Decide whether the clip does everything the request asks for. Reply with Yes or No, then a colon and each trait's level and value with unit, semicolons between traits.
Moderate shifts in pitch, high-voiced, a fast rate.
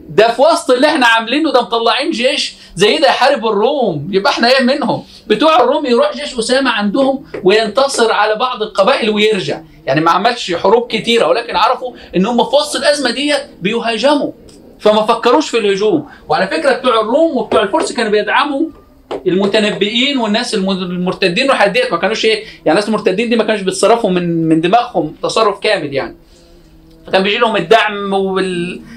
Yes: average, 4.6 semitones; high, 230 Hz; fast, 165 wpm